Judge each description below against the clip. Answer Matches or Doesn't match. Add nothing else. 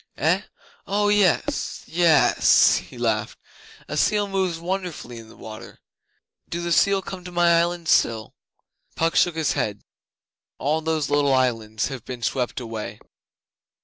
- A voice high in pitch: Doesn't match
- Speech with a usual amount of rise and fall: Doesn't match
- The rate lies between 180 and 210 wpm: Doesn't match